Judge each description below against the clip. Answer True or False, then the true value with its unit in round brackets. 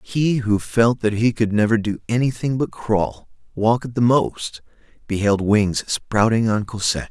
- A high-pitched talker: False (110 Hz)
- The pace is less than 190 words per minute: True (170 wpm)